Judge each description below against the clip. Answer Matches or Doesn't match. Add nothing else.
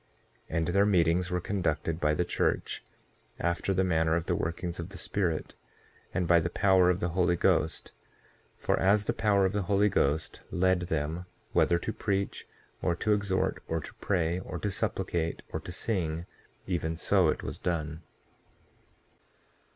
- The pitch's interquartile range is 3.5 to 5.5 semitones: Doesn't match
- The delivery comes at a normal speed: Matches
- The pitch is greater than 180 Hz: Doesn't match